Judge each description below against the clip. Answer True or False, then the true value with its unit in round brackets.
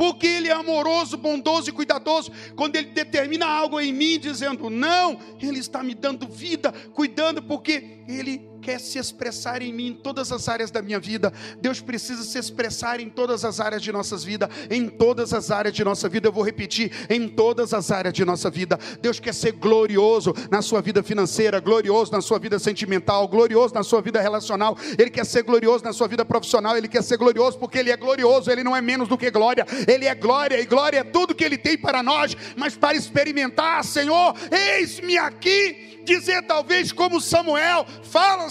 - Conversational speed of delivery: False (200 wpm)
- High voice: True (245 Hz)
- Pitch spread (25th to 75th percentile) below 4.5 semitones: False (5.2 semitones)